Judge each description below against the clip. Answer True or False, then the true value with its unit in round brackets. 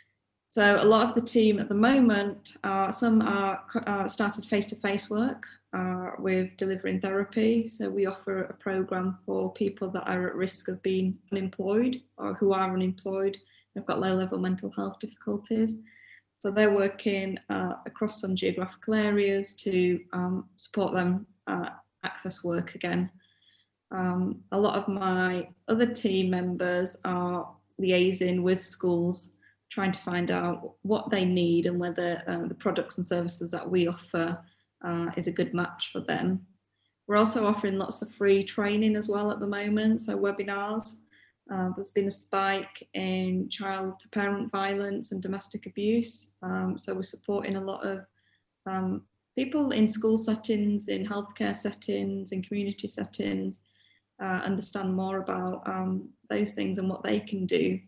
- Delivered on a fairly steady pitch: True (2.1 semitones)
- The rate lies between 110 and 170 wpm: True (160 wpm)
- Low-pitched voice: False (195 Hz)